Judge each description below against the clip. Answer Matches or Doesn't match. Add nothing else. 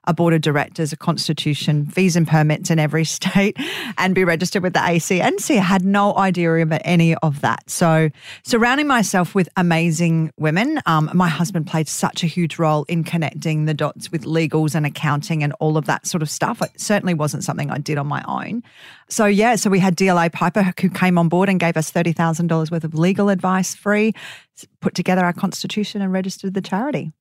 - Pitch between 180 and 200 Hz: Doesn't match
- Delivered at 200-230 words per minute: Matches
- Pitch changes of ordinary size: Matches